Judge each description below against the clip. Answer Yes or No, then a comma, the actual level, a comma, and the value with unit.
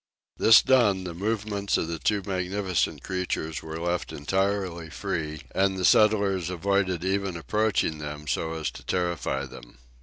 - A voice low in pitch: Yes, very low, 90 Hz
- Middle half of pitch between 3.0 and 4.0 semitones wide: Yes, average, 3.6 semitones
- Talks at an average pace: Yes, average, 150 wpm